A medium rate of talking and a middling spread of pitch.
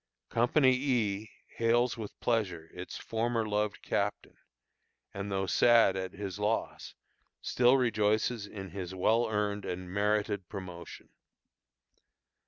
No: slow, 115 wpm; average, 3.1 semitones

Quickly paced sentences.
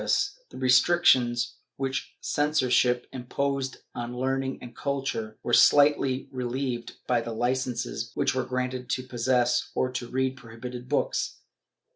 No: average, 145 wpm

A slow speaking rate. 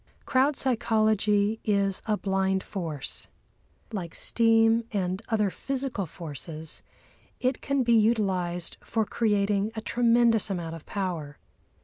Yes: slow, 115 wpm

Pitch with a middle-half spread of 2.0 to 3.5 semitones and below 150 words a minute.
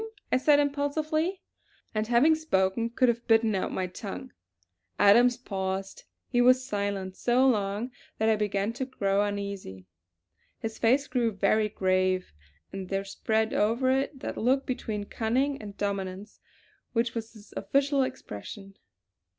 No: average, 4.5 semitones; average, 140 wpm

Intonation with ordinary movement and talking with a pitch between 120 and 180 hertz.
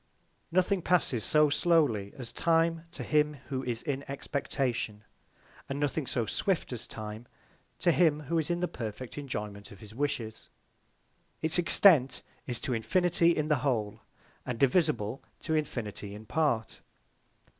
No: wide, 6.1 semitones; medium, 140 Hz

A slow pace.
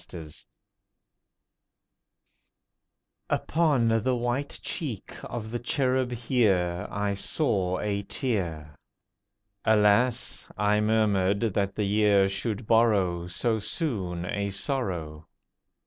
Yes: slow, 95 wpm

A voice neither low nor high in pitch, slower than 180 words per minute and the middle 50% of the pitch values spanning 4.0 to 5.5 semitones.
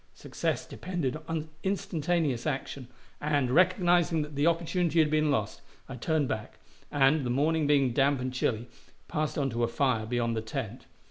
Yes: medium, 145 Hz; average, 170 wpm; average, 4.3 semitones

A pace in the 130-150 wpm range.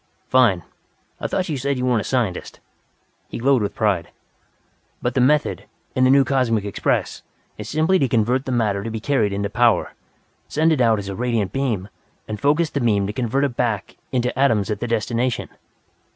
No: average, 195 wpm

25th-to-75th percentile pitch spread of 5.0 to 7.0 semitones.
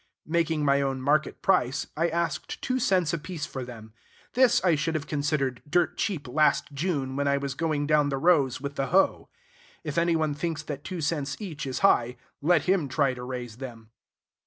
No: average, 3.7 semitones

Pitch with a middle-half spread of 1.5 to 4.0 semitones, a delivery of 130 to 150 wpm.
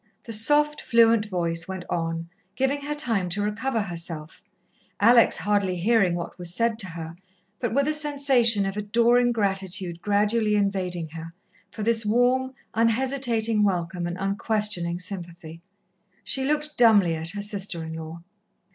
No: average, 5.0 semitones; average, 145 wpm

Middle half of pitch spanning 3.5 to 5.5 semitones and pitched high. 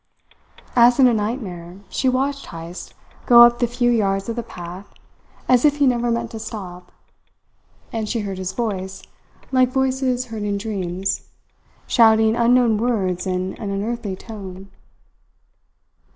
Yes: average, 4.0 semitones; high, 220 Hz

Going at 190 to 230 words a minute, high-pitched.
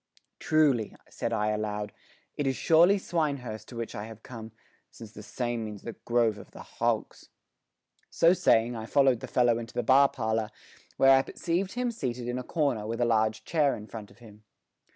No: average, 195 wpm; low, 120 Hz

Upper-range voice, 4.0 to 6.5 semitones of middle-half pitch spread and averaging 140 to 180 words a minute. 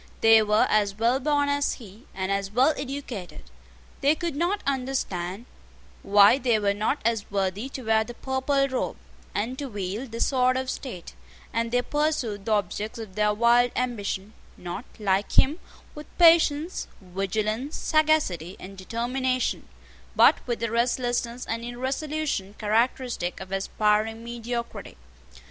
Yes: high, 235 Hz; average, 4.3 semitones; average, 145 wpm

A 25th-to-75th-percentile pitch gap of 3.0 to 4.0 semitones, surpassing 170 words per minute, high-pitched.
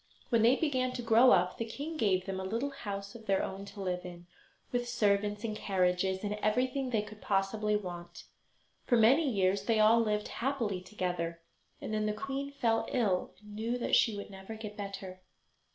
Yes: average, 3.4 semitones; average, 190 wpm; high, 210 Hz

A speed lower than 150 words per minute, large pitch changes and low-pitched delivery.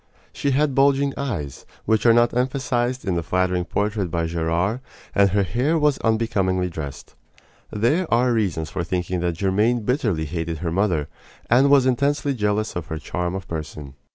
No: average, 170 wpm; wide, 6.4 semitones; low, 105 Hz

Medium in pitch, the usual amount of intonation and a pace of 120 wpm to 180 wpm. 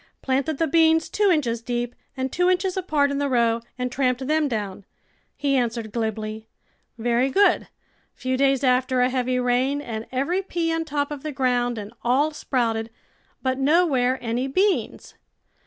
No: very high, 260 Hz; average, 3.9 semitones; average, 170 wpm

